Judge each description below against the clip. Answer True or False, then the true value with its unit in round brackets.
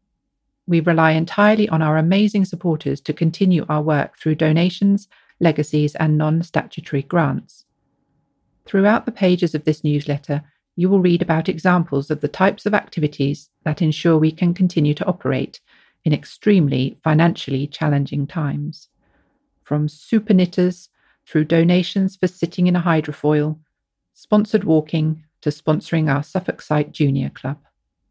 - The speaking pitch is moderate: True (160 Hz)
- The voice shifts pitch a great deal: False (3.2 semitones)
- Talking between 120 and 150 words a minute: True (140 wpm)